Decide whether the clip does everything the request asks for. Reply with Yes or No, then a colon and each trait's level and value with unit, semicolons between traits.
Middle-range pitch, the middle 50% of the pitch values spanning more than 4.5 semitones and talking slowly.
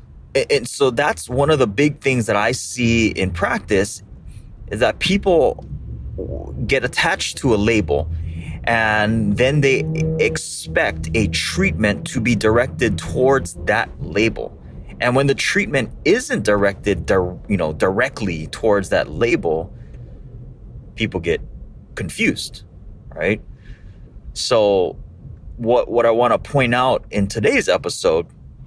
No: low, 110 Hz; average, 5.1 semitones; slow, 125 wpm